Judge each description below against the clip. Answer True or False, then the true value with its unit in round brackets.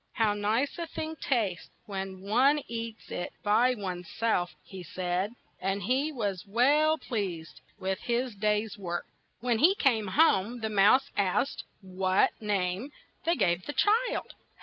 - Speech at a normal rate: True (150 wpm)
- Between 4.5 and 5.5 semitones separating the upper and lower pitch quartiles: True (5.0 semitones)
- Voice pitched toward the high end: True (210 Hz)